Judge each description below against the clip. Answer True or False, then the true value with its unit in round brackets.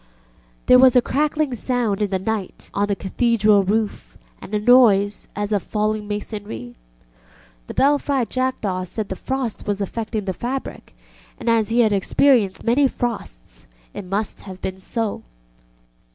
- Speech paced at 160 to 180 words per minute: False (150 wpm)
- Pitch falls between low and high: False (215 Hz)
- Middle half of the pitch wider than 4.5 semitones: False (3.6 semitones)